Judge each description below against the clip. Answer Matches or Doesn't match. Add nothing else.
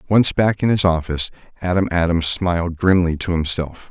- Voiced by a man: Matches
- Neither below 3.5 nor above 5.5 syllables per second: Matches